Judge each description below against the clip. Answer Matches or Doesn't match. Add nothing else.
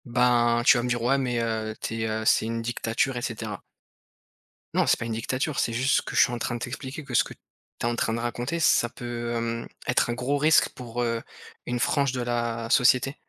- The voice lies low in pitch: Matches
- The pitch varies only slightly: Matches